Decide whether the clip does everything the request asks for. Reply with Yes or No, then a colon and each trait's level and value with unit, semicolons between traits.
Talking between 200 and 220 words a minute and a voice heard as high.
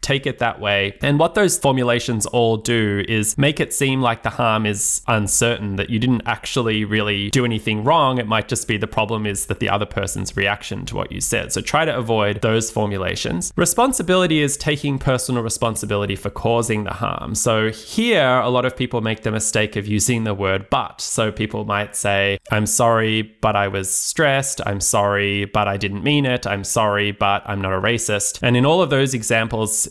No: fast, 205 wpm; low, 110 Hz